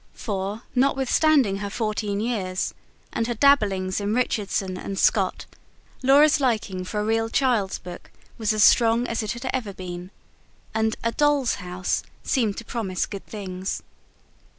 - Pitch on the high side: Yes, high, 215 Hz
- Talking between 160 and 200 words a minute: No, average, 150 wpm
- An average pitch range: Yes, average, 3.9 semitones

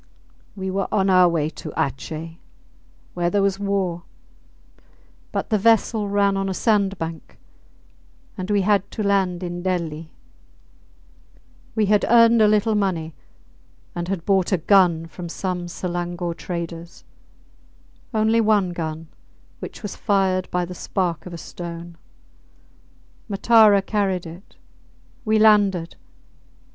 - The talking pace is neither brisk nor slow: No, slow, 130 wpm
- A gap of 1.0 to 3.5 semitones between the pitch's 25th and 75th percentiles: Yes, average, 2.9 semitones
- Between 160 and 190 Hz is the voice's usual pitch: Yes, medium, 185 Hz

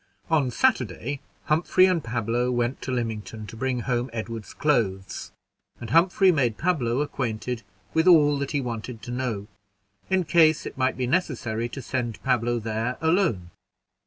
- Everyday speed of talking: Yes, average, 155 wpm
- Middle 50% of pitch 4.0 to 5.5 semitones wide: Yes, average, 4.5 semitones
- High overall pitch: No, low, 125 Hz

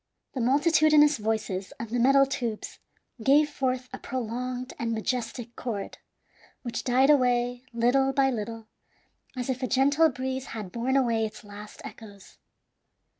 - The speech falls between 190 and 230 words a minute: No, average, 140 wpm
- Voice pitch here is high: Yes, very high, 250 Hz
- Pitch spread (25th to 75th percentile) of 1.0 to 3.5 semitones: Yes, average, 2.8 semitones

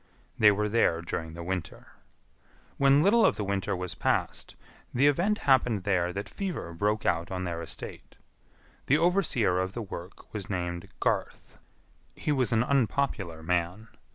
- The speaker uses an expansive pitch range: Yes, wide, 6.9 semitones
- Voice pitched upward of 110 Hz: No, low, 100 Hz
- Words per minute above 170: No, average, 155 wpm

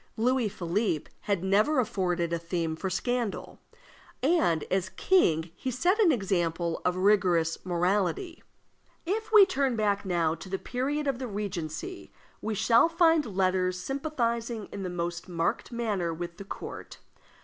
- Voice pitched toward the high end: Yes, high, 200 Hz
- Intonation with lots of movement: Yes, wide, 6.5 semitones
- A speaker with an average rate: Yes, average, 150 wpm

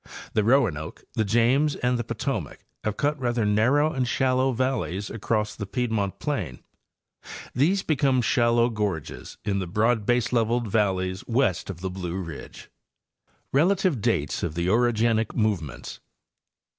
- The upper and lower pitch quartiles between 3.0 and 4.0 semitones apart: No, average, 4.4 semitones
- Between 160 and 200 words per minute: No, slow, 135 wpm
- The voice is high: No, low, 115 Hz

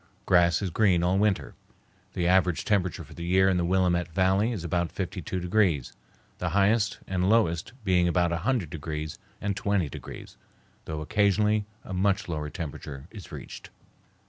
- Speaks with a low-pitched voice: Yes, very low, 90 Hz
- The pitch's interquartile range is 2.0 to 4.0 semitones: Yes, average, 2.9 semitones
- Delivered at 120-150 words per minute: No, average, 160 wpm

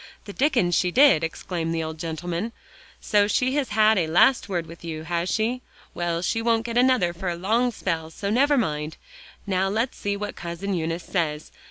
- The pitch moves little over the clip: No, average, 5.2 semitones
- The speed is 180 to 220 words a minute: Yes, average, 195 wpm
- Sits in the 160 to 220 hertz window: Yes, medium, 185 Hz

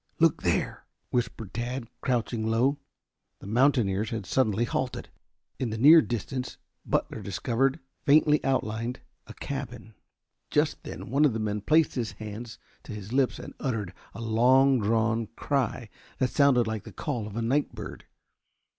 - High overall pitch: No, low, 120 Hz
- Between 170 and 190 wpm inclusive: No, average, 155 wpm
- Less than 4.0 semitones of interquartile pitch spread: Yes, average, 3.3 semitones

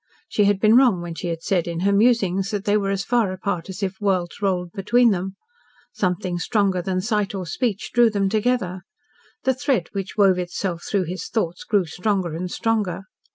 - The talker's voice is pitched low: No, high, 195 Hz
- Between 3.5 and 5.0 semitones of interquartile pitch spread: No, average, 2.8 semitones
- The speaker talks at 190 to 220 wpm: Yes, average, 200 wpm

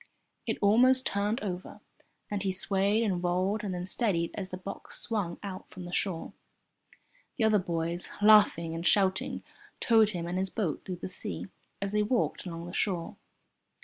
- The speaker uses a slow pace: No, average, 175 wpm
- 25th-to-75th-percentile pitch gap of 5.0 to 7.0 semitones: No, average, 2.9 semitones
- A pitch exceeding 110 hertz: Yes, high, 190 Hz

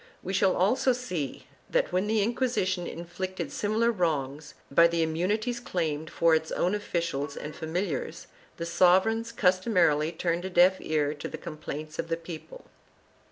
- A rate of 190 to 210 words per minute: No, average, 155 wpm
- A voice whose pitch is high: No, medium, 175 Hz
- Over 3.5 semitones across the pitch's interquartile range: Yes, average, 4.1 semitones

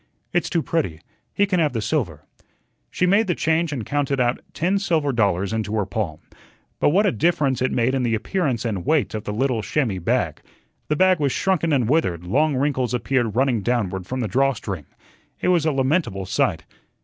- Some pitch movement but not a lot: No, wide, 6.5 semitones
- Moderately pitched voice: No, low, 130 Hz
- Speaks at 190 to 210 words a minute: Yes, average, 200 wpm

